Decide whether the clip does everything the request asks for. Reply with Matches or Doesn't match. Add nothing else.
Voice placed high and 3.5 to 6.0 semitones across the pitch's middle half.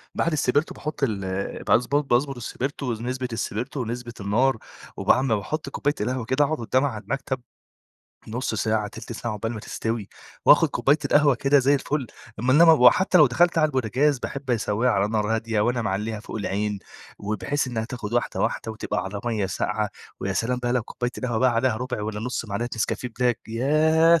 Doesn't match